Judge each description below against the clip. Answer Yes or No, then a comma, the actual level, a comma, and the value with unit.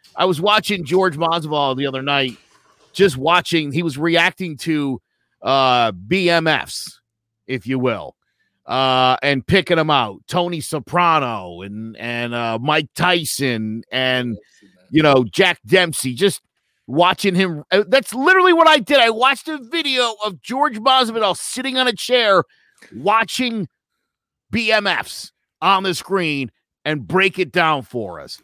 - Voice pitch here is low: No, medium, 170 Hz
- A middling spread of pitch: No, wide, 7.2 semitones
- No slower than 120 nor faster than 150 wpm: Yes, average, 140 wpm